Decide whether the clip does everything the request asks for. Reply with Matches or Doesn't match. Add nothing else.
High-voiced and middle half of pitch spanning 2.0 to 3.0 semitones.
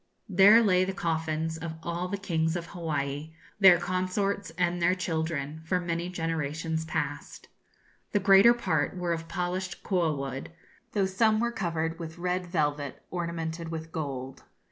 Doesn't match